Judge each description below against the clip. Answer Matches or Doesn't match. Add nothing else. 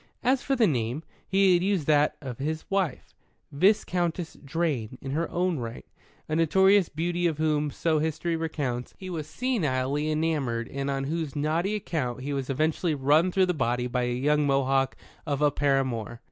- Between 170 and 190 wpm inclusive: Matches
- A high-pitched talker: Doesn't match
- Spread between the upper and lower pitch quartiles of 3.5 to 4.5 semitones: Matches